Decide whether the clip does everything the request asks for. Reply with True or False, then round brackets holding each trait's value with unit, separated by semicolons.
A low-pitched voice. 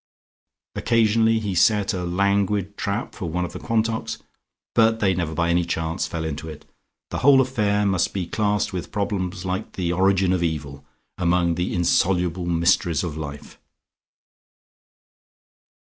True (90 Hz)